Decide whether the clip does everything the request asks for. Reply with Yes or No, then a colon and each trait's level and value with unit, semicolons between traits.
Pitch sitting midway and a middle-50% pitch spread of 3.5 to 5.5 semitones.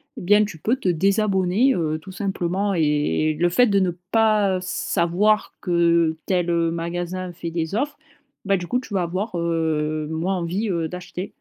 No: medium, 180 Hz; average, 2.9 semitones